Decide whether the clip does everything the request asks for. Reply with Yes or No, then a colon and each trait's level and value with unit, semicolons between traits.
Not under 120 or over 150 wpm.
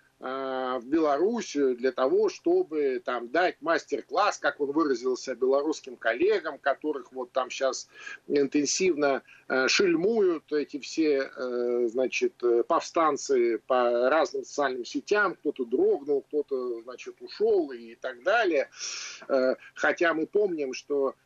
No: slow, 110 wpm